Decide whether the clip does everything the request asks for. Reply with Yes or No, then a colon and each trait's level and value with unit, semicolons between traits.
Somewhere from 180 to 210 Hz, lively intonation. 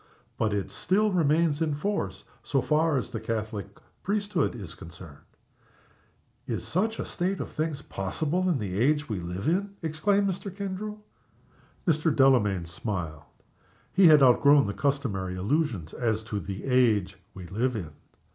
No: low, 135 Hz; wide, 8.6 semitones